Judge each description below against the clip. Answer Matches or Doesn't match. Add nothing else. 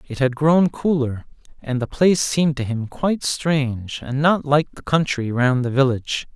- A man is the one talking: Matches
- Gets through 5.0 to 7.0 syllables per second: Doesn't match